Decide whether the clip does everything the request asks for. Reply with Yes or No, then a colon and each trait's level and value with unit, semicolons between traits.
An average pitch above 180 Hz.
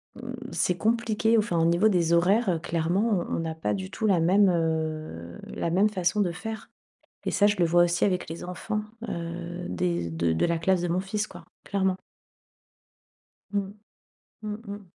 No: medium, 175 Hz